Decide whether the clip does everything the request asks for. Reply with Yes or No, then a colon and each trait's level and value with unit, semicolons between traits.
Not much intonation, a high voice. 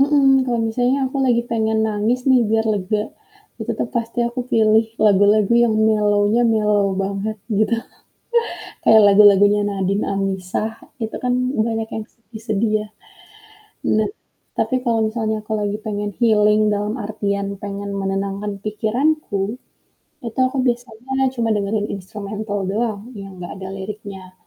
Yes: narrow, 2.2 semitones; high, 215 Hz